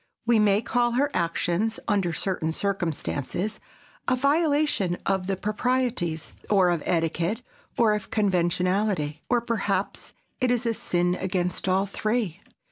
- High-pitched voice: Yes, high, 195 Hz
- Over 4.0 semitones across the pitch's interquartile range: Yes, average, 4.7 semitones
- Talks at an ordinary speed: No, slow, 130 wpm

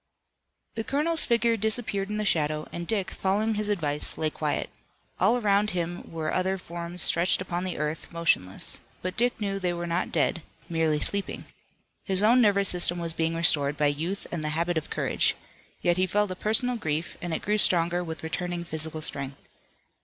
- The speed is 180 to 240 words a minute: Yes, average, 185 wpm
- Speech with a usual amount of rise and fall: Yes, average, 4.0 semitones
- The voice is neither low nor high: Yes, medium, 175 Hz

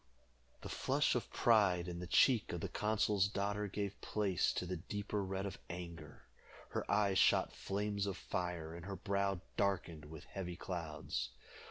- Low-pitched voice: Yes, very low, 95 Hz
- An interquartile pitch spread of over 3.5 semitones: No, narrow, 2.5 semitones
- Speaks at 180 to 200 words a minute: No, average, 165 wpm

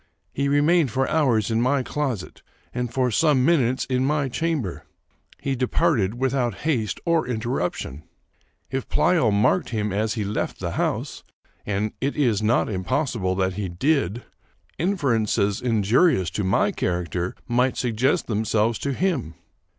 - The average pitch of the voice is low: Yes, low, 120 Hz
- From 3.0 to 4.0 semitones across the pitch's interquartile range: No, average, 5.0 semitones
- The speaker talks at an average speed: Yes, average, 150 wpm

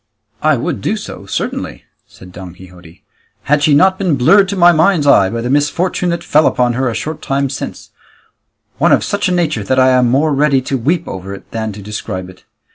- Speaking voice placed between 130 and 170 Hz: Yes, low, 135 Hz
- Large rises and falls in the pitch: Yes, wide, 6.9 semitones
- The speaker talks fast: Yes, fast, 215 wpm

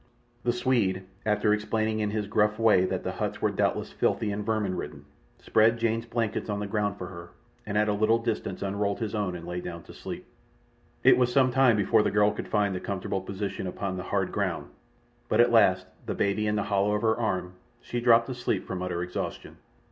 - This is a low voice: Yes, low, 105 Hz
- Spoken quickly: Yes, fast, 215 wpm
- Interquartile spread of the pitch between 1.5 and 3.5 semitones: Yes, average, 2.9 semitones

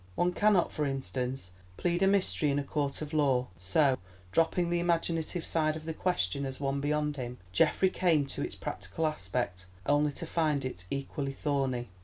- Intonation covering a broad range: No, average, 3.6 semitones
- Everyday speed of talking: Yes, average, 180 wpm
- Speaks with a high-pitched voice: No, medium, 145 Hz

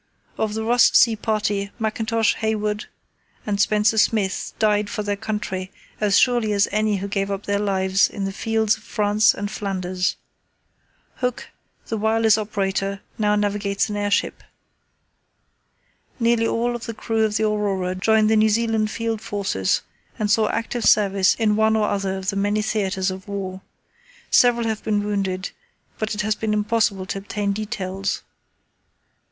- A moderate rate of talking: Yes, average, 160 wpm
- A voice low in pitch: No, high, 210 Hz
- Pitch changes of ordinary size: No, narrow, 1.7 semitones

